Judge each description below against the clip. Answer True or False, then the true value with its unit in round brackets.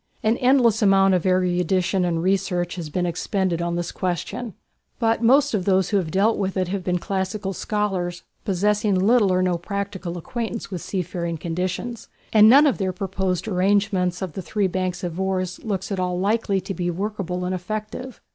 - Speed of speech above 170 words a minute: True (180 wpm)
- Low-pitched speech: False (190 Hz)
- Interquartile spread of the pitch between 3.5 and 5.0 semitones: False (2.6 semitones)